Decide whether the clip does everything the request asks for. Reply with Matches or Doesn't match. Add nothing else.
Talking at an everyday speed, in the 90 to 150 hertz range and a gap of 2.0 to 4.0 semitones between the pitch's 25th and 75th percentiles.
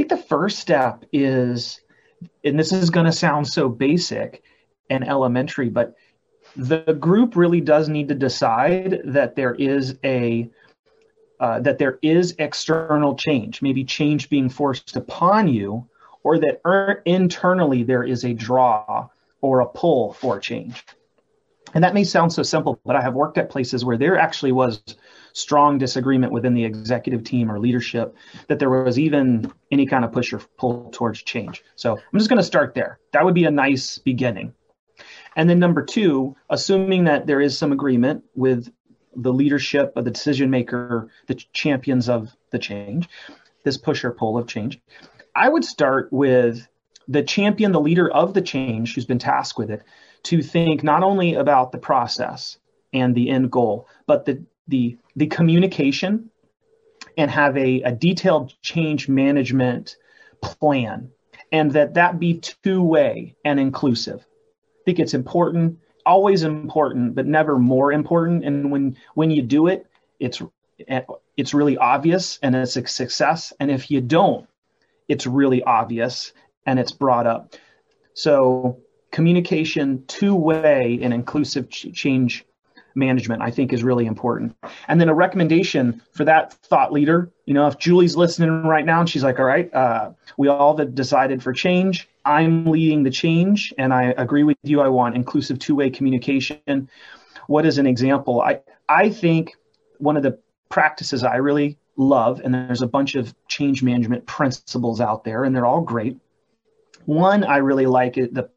Doesn't match